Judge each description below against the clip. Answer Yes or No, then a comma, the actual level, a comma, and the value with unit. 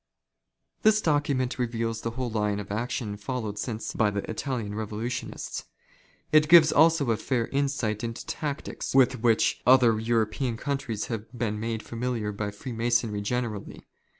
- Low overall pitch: Yes, low, 115 Hz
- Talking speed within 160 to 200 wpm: No, average, 145 wpm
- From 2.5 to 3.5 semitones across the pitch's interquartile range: Yes, average, 3.1 semitones